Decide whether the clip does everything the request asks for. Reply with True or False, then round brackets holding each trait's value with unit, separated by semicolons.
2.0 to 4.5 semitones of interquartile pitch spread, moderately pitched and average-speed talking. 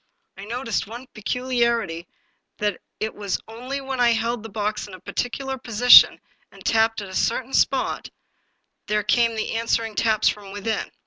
False (2.6 semitones; 225 Hz; 165 wpm)